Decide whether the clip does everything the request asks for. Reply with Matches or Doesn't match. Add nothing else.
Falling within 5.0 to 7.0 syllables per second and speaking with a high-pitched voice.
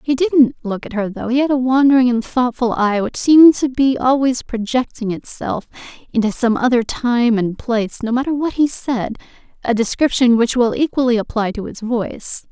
Matches